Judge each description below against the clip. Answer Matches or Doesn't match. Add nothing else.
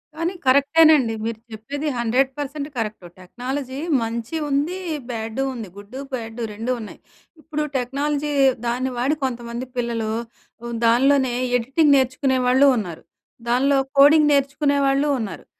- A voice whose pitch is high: Matches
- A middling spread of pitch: Matches